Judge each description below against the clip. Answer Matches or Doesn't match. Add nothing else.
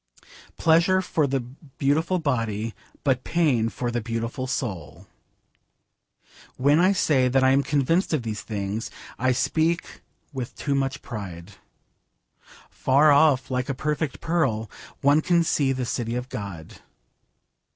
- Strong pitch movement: Doesn't match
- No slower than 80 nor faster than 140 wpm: Matches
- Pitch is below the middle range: Matches